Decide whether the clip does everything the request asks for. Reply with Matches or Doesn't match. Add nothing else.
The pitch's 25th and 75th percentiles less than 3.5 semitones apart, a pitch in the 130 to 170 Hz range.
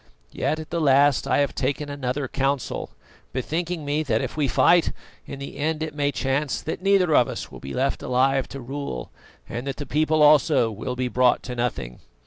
Matches